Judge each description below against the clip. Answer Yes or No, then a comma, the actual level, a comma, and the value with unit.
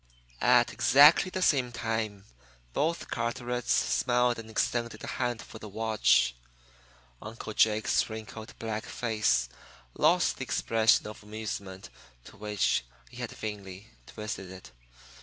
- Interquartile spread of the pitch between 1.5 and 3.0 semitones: Yes, narrow, 2.4 semitones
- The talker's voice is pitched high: No, low, 110 Hz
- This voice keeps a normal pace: No, slow, 125 wpm